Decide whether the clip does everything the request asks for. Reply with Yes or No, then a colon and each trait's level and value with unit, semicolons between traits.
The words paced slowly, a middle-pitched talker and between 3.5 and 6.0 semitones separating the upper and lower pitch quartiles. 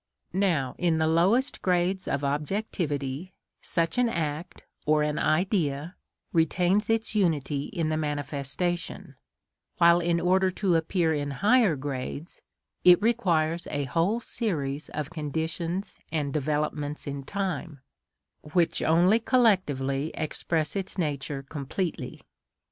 Yes: slow, 120 wpm; medium, 165 Hz; average, 4.2 semitones